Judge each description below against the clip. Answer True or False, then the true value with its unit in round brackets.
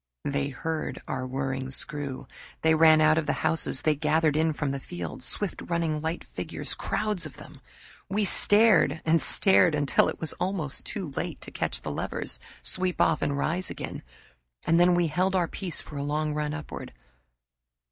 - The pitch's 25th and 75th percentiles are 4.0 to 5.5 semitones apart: False (3.2 semitones)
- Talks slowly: False (180 wpm)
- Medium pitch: True (155 Hz)